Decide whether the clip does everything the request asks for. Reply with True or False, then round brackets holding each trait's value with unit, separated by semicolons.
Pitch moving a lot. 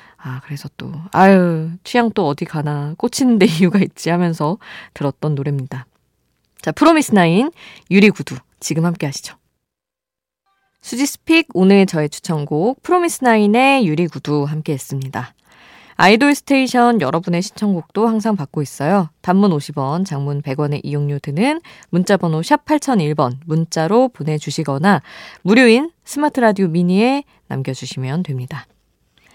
True (7.5 semitones)